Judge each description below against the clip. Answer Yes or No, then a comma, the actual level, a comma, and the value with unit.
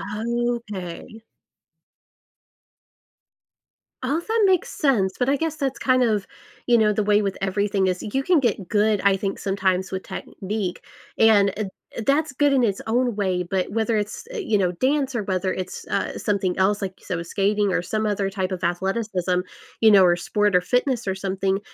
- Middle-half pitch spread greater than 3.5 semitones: Yes, average, 3.9 semitones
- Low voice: No, high, 205 Hz